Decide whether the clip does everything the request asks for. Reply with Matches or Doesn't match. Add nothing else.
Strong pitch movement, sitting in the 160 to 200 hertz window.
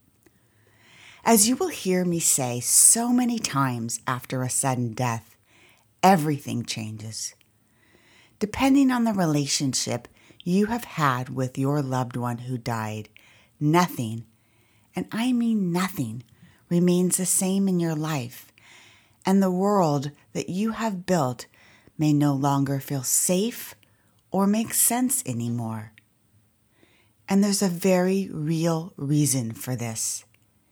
Doesn't match